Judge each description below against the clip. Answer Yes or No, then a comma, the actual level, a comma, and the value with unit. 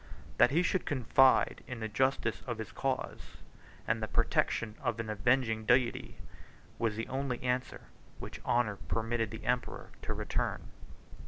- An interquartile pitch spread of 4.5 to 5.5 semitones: No, narrow, 2.5 semitones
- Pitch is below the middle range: Yes, low, 120 Hz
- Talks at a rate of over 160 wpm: No, average, 150 wpm